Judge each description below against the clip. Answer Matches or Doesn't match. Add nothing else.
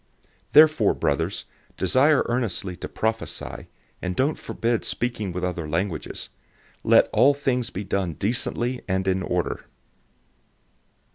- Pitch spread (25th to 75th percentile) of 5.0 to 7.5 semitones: Matches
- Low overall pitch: Matches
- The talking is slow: Matches